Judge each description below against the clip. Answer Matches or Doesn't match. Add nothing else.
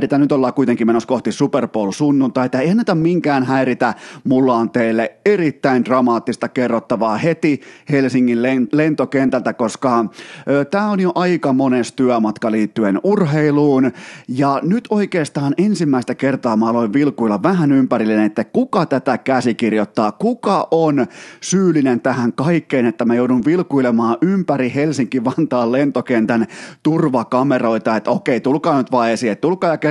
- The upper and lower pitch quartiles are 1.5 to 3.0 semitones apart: Doesn't match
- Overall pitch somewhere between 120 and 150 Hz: Matches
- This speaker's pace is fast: Doesn't match